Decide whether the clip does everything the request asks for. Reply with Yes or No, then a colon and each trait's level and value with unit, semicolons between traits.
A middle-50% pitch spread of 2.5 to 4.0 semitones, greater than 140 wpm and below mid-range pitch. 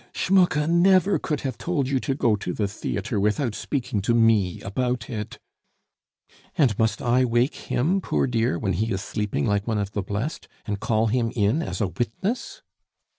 No: average, 5.1 semitones; average, 185 wpm; low, 115 Hz